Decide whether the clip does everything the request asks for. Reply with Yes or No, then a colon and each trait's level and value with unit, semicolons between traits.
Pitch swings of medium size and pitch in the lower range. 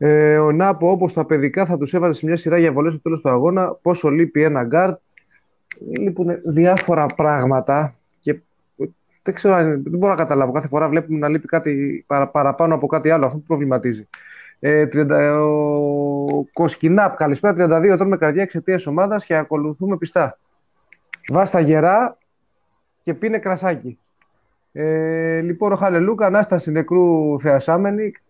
No: average, 3.4 semitones; medium, 160 Hz